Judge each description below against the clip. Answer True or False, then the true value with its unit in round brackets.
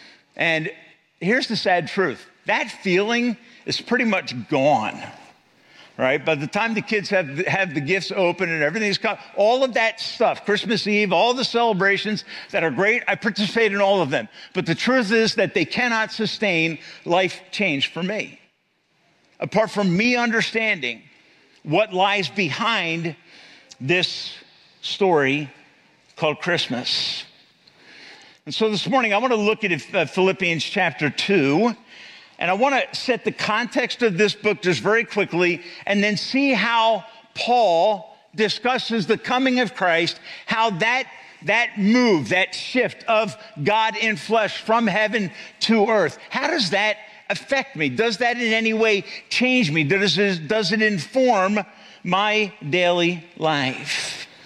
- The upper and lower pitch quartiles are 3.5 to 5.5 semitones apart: True (4.0 semitones)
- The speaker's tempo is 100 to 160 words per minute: True (150 wpm)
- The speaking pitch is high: True (210 Hz)